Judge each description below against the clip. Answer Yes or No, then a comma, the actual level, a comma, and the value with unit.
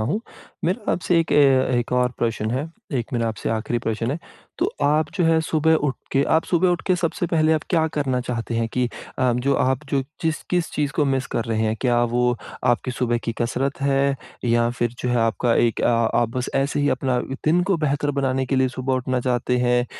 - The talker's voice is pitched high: No, low, 130 Hz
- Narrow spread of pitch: No, average, 3.9 semitones